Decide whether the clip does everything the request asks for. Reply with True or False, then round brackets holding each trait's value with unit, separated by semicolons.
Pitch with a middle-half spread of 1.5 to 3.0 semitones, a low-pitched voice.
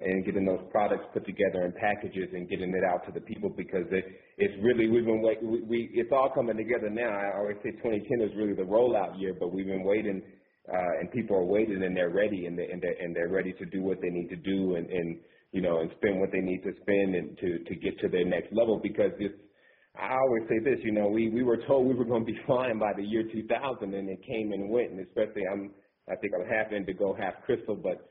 True (2.7 semitones; 100 Hz)